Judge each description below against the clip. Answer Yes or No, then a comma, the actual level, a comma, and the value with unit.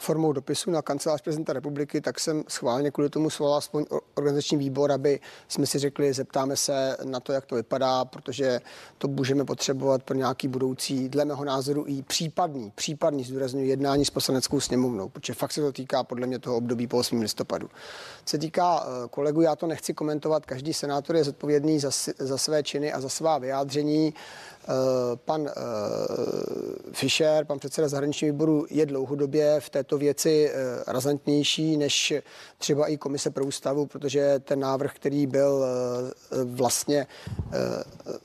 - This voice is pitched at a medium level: Yes, medium, 145 Hz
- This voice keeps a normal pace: Yes, average, 160 wpm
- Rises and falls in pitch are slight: Yes, narrow, 2.2 semitones